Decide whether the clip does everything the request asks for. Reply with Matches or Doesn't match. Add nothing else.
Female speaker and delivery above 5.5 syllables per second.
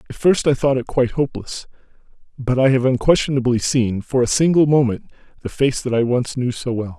Doesn't match